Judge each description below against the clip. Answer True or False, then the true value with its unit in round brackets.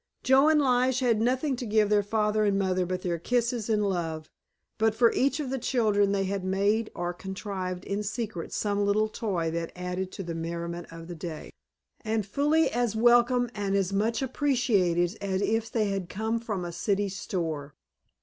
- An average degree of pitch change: True (4.2 semitones)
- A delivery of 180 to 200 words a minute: True (190 wpm)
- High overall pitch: True (205 Hz)